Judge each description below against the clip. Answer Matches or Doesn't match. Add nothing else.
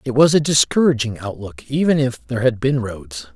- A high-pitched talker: Doesn't match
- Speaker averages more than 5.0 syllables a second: Matches